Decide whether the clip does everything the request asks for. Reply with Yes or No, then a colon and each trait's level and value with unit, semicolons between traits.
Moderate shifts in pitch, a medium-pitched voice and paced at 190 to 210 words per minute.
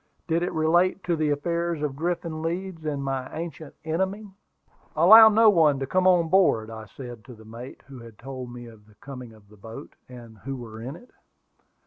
No: wide, 6.1 semitones; medium, 145 Hz; average, 200 wpm